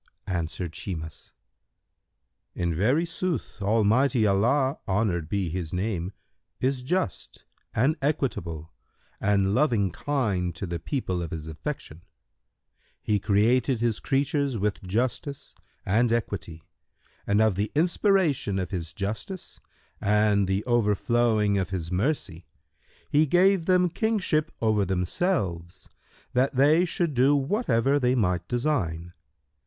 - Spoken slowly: Yes, slow, 120 wpm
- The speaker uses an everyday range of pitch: No, wide, 7.1 semitones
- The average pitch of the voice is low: Yes, low, 110 Hz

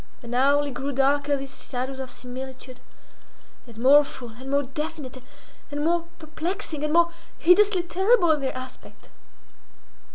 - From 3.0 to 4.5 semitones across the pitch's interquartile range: Yes, average, 3.6 semitones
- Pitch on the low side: No, very high, 285 Hz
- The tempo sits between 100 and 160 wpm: Yes, average, 140 wpm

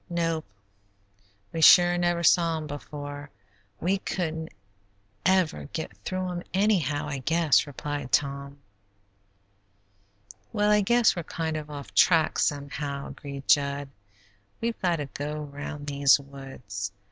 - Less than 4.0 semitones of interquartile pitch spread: Yes, average, 3.5 semitones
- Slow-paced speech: Yes, slow, 130 wpm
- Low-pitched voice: No, medium, 150 Hz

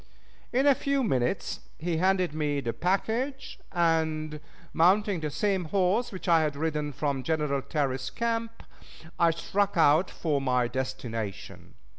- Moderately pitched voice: Yes, medium, 160 Hz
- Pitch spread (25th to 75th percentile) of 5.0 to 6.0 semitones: Yes, wide, 5.4 semitones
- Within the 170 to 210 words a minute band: No, average, 140 wpm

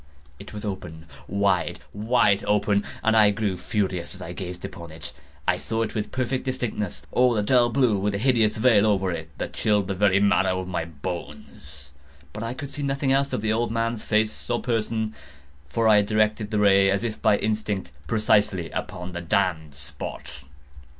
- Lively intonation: No, average, 3.5 semitones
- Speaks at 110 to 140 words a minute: No, average, 185 wpm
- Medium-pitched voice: No, low, 105 Hz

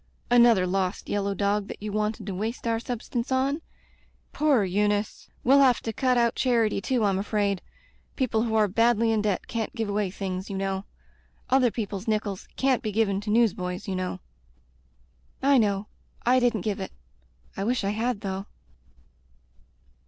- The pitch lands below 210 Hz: No, high, 215 Hz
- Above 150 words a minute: Yes, average, 170 wpm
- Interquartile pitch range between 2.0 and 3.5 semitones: Yes, average, 3.2 semitones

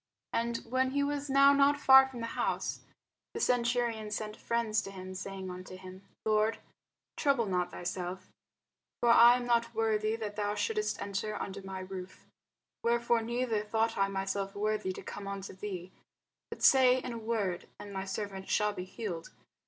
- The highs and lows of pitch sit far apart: No, average, 3.6 semitones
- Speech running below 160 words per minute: No, average, 170 wpm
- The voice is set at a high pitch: Yes, high, 215 Hz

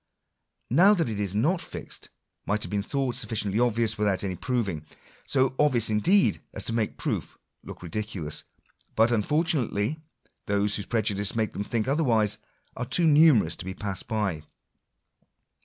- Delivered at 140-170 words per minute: Yes, average, 160 wpm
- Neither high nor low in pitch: No, low, 110 Hz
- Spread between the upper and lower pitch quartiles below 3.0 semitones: No, average, 4.3 semitones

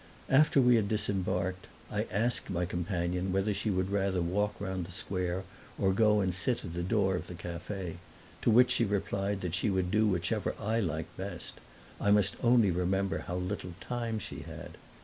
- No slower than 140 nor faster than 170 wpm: No, average, 190 wpm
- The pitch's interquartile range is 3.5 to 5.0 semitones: No, narrow, 2.5 semitones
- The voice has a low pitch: Yes, very low, 95 Hz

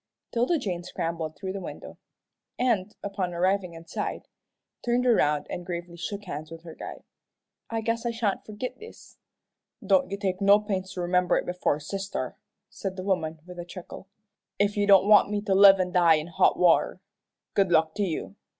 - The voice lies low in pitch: No, high, 190 Hz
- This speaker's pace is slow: No, average, 185 wpm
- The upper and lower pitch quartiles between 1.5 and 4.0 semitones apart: Yes, average, 2.9 semitones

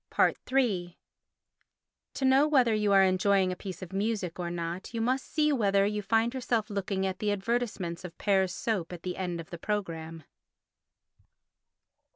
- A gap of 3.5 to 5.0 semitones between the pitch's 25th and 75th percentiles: Yes, average, 4.0 semitones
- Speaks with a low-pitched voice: No, high, 195 Hz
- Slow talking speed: No, average, 165 wpm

